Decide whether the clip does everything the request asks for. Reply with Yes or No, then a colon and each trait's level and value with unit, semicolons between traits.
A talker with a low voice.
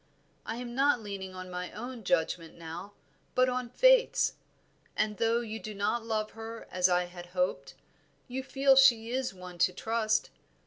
No: high, 220 Hz